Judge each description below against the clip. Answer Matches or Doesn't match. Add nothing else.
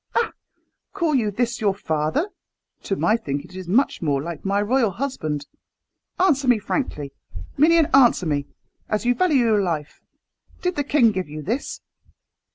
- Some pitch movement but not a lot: Doesn't match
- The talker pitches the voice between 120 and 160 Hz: Doesn't match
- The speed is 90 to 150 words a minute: Doesn't match